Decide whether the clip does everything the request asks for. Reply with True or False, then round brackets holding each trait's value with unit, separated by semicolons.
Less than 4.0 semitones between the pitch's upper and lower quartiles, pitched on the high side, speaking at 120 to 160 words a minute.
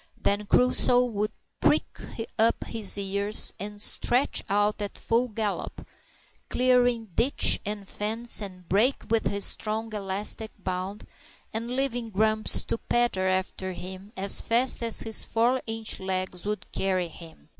True (2.9 semitones; 210 Hz; 140 wpm)